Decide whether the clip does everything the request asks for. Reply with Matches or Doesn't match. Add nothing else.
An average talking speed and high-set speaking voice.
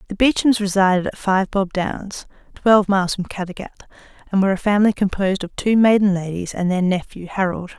Matches